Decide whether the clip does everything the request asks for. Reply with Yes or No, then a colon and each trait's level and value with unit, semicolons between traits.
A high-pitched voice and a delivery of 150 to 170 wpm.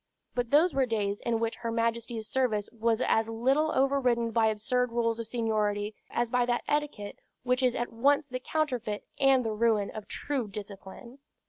No: high, 235 Hz; average, 180 wpm